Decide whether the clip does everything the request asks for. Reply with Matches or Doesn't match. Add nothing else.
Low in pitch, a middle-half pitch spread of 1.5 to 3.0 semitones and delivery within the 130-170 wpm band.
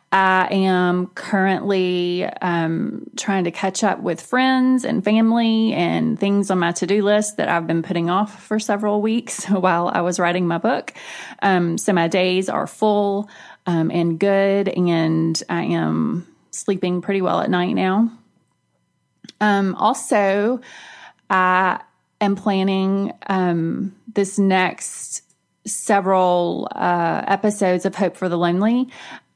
Doesn't match